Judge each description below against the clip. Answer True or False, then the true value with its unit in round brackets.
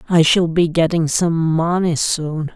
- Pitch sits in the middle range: True (165 Hz)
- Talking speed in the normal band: True (165 wpm)